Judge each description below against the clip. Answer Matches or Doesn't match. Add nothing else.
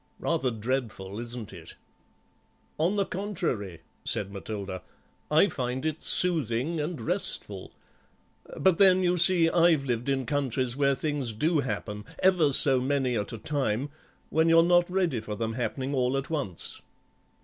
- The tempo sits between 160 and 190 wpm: Doesn't match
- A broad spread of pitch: Matches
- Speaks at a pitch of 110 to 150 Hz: Matches